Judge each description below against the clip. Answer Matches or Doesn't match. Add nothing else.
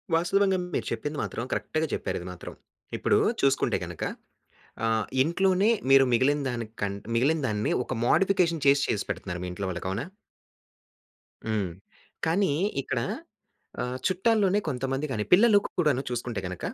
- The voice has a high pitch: Doesn't match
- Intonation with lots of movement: Matches